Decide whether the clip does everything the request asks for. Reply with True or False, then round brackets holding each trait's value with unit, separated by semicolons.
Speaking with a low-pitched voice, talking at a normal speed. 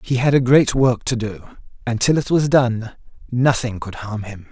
False (120 Hz; 215 wpm)